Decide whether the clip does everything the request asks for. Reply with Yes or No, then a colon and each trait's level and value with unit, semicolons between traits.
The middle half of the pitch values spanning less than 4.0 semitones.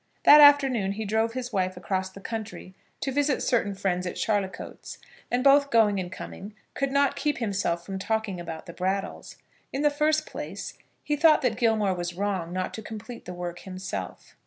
No: wide, 5.5 semitones